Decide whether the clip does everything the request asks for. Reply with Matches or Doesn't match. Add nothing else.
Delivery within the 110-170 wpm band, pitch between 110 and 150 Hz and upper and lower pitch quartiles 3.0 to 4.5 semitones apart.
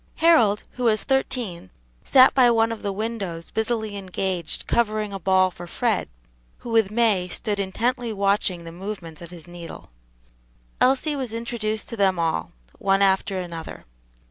Doesn't match